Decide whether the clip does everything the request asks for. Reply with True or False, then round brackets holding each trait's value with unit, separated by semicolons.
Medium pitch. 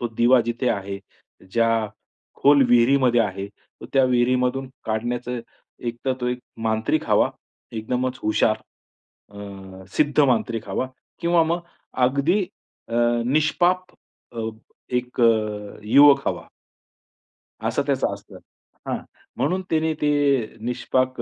False (125 Hz)